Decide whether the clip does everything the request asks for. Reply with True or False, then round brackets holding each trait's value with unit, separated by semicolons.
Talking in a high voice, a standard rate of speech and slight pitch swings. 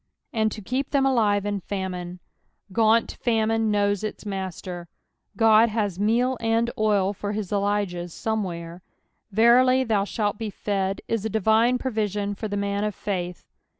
True (210 Hz; 165 wpm; 2.3 semitones)